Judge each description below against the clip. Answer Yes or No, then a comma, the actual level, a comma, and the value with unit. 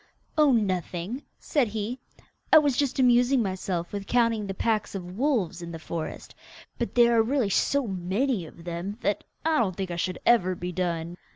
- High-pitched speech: Yes, high, 205 Hz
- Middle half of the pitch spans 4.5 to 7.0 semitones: Yes, average, 5.3 semitones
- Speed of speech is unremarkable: Yes, average, 185 wpm